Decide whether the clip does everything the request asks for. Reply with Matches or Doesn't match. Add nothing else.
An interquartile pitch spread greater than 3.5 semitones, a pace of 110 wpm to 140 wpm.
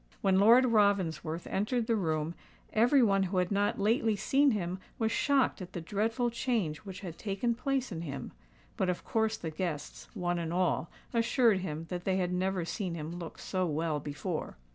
Doesn't match